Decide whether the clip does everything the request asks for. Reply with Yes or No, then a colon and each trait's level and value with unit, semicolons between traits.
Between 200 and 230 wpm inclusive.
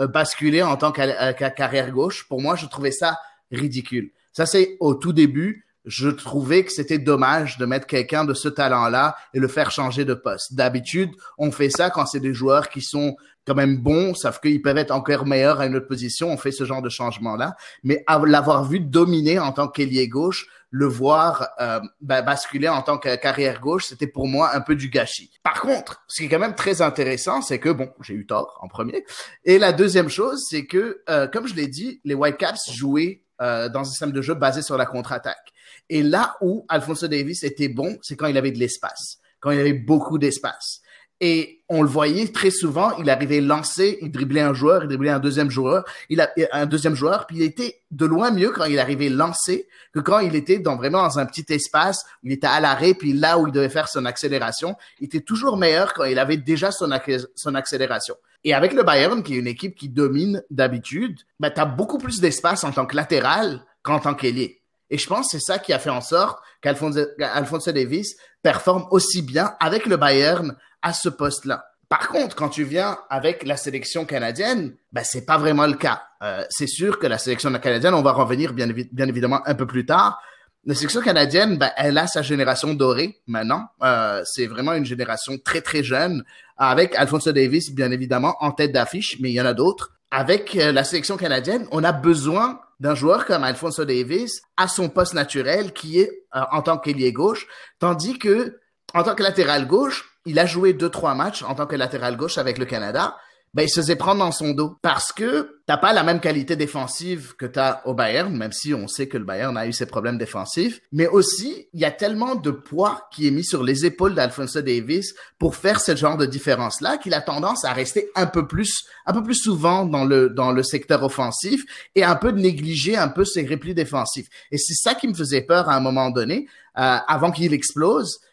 Yes: fast, 220 wpm